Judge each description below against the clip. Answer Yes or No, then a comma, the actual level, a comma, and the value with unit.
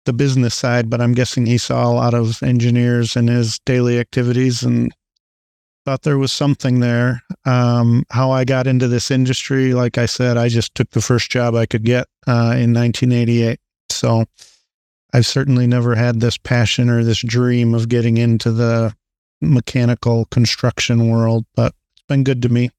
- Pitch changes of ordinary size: No, narrow, 1.3 semitones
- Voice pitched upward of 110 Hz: Yes, low, 120 Hz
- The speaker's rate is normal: Yes, average, 175 wpm